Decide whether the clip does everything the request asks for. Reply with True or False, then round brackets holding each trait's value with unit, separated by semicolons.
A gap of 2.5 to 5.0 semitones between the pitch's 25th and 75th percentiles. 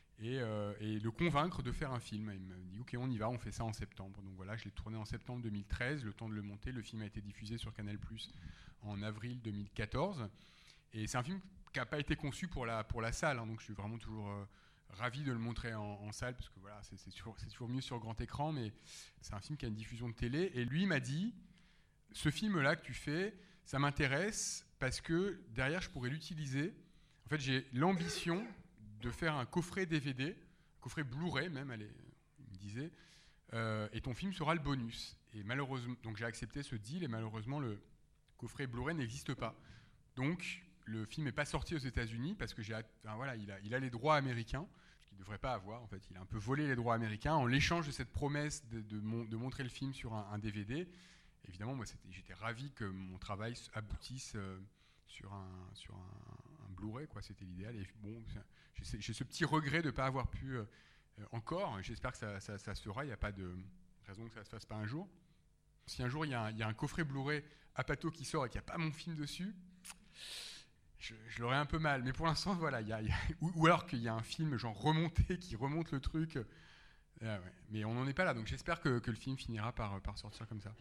False (5.6 semitones)